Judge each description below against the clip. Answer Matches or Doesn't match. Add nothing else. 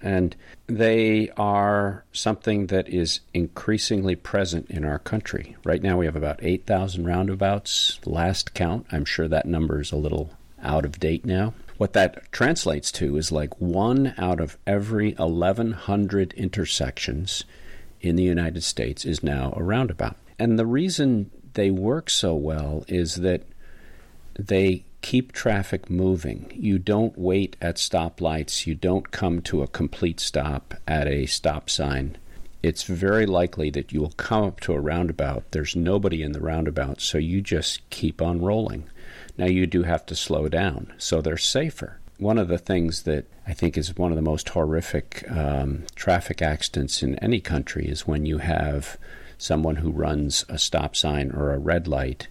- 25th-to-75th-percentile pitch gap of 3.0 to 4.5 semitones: Matches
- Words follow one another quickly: Doesn't match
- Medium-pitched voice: Doesn't match